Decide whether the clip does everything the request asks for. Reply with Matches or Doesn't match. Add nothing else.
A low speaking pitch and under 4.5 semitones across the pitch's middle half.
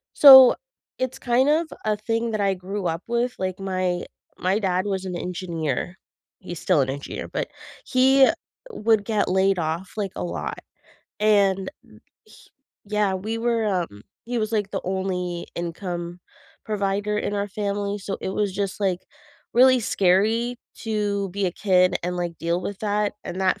Doesn't match